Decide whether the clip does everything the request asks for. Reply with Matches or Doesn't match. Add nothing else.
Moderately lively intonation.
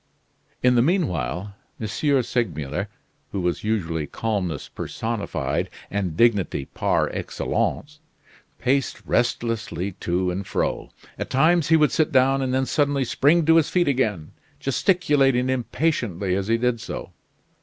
Doesn't match